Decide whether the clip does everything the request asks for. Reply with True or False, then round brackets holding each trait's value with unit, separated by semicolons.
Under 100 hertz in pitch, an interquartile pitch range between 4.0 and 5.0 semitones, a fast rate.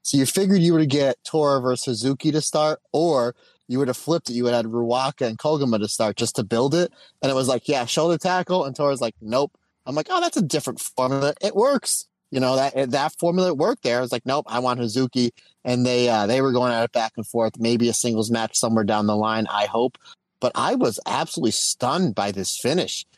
False (130 Hz; 4.3 semitones; 245 wpm)